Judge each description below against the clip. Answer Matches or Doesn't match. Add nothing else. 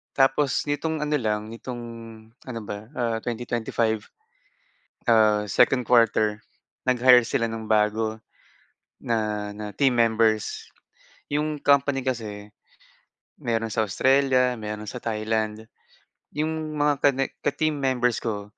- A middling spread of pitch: Matches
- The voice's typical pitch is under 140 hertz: Matches